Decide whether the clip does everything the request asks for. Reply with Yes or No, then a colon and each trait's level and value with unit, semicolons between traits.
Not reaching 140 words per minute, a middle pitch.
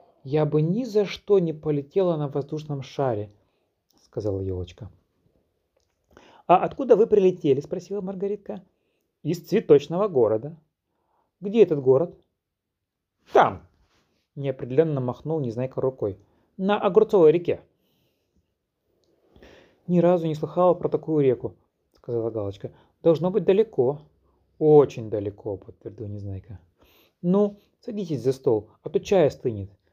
Yes: slow, 110 wpm; medium, 145 Hz